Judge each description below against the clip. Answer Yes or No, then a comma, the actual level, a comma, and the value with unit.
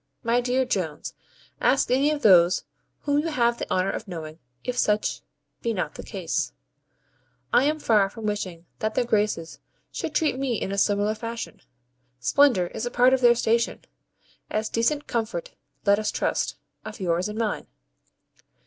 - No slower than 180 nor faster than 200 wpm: No, average, 165 wpm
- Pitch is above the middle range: Yes, high, 225 Hz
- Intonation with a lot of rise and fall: No, average, 3.8 semitones